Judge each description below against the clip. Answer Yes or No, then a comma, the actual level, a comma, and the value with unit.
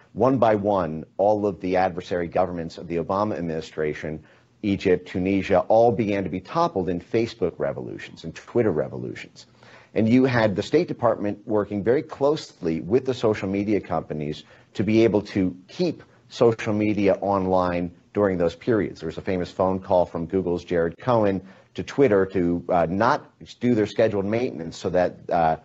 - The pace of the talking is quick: No, average, 170 wpm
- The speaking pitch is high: No, very low, 95 Hz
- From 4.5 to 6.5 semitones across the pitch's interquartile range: No, average, 3.8 semitones